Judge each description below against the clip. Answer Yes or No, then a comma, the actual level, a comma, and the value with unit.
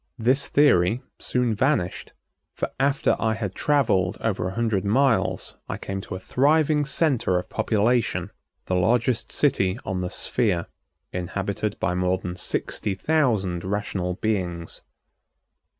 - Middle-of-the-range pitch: No, low, 105 Hz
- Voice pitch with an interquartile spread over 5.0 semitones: Yes, wide, 5.5 semitones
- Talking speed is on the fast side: No, slow, 135 wpm